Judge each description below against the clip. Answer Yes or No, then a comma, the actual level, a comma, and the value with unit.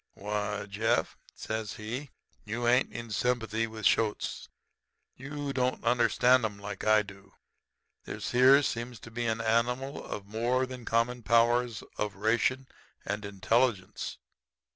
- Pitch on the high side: No, low, 115 Hz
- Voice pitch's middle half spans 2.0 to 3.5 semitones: Yes, average, 2.7 semitones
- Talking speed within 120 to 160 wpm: Yes, average, 140 wpm